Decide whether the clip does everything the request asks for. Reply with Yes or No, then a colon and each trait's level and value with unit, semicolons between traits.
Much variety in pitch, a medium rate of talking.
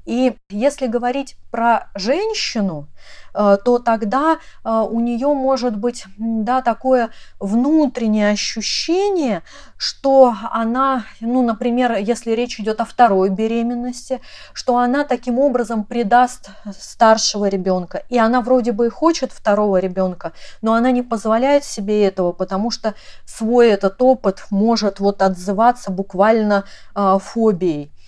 No: average, 3.5 semitones; average, 120 wpm